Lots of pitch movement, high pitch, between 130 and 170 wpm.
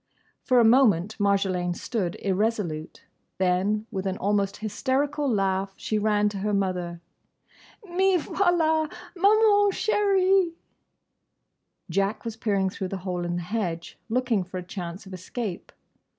Yes: wide, 5.9 semitones; high, 205 Hz; slow, 135 wpm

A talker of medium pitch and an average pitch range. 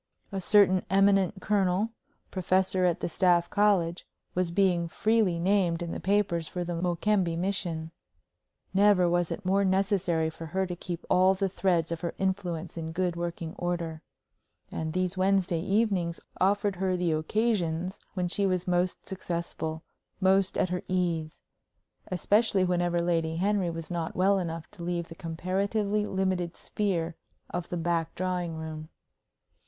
No: medium, 180 Hz; narrow, 2.3 semitones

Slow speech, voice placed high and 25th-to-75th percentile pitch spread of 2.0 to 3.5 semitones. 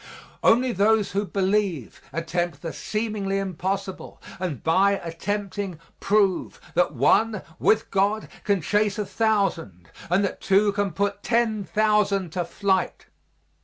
Yes: slow, 130 wpm; high, 195 Hz; average, 2.9 semitones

